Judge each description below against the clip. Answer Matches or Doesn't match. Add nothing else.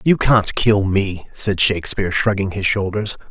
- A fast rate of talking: Doesn't match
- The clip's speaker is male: Matches